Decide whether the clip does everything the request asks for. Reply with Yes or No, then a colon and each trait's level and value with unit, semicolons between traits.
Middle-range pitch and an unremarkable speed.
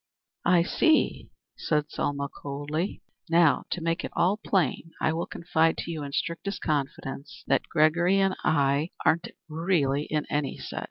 Yes: medium, 160 Hz; average, 155 wpm